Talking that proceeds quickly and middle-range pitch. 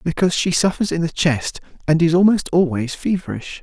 No: average, 180 wpm; medium, 165 Hz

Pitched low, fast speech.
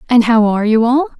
No: high, 230 Hz; fast, 250 wpm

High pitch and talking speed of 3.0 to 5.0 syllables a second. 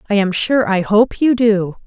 Yes: high, 205 Hz; 4.4 syllables/s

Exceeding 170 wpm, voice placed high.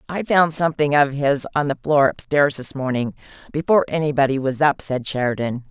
No: average, 190 wpm; medium, 140 Hz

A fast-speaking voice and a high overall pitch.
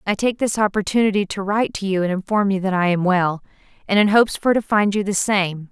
Yes: fast, 250 wpm; high, 200 Hz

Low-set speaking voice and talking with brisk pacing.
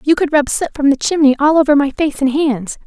No: very high, 285 Hz; fast, 275 wpm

